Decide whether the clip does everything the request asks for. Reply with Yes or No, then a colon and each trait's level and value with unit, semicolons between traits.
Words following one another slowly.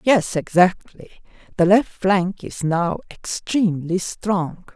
Yes: slow, 115 wpm